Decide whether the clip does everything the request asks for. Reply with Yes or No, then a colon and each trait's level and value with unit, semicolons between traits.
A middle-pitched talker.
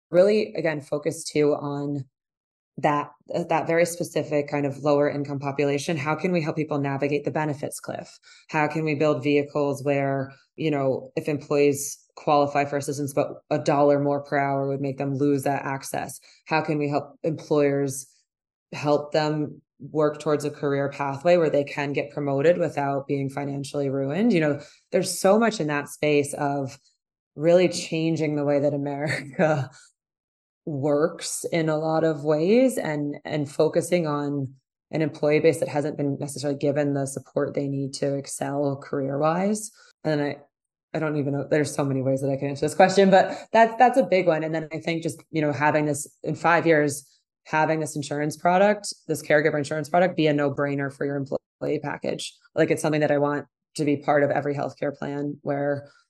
Yes: medium, 145 Hz